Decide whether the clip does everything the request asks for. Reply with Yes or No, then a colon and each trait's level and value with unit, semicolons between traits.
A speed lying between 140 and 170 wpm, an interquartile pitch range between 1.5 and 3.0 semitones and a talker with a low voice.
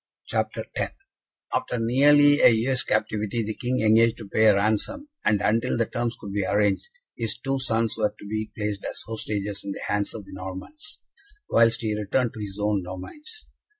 No: average, 185 wpm; narrow, 2.6 semitones; low, 110 Hz